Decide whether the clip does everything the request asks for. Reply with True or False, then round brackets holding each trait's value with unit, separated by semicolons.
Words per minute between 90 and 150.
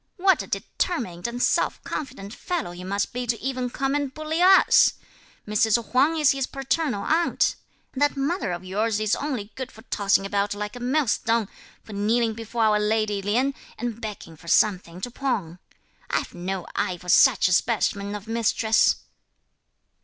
False (170 wpm)